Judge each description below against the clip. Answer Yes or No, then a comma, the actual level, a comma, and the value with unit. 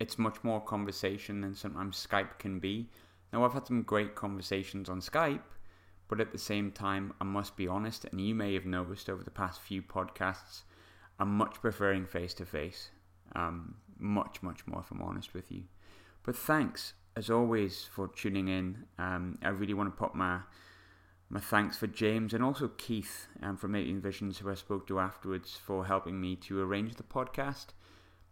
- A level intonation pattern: Yes, narrow, 2.1 semitones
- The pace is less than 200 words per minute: Yes, average, 185 wpm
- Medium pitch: No, very low, 95 Hz